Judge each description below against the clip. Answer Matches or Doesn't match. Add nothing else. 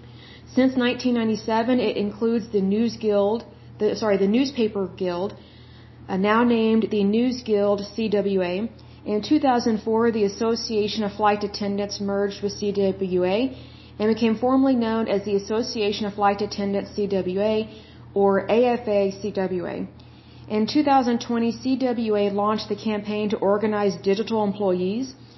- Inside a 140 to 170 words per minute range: Doesn't match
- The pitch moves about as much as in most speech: Doesn't match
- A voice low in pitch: Doesn't match